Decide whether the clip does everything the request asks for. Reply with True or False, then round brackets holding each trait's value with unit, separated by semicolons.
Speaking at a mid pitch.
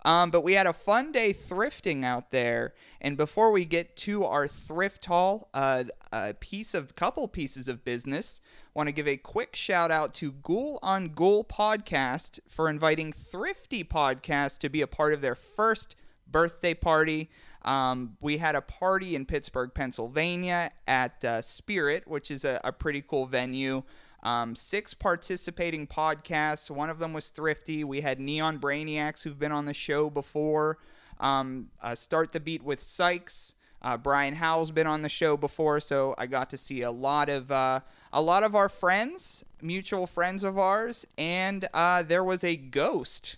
True (155 Hz)